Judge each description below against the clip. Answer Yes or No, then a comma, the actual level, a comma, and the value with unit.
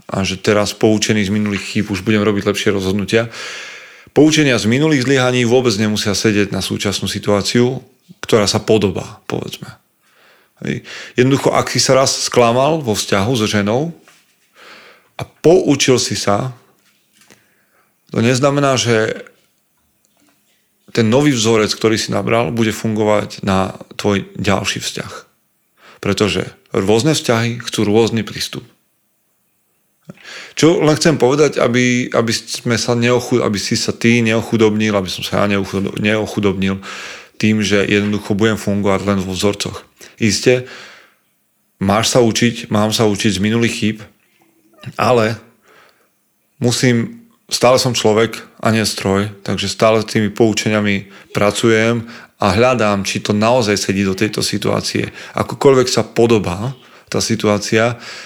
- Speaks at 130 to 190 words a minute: Yes, average, 135 wpm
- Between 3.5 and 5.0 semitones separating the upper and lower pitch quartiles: No, average, 2.9 semitones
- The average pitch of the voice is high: No, low, 110 Hz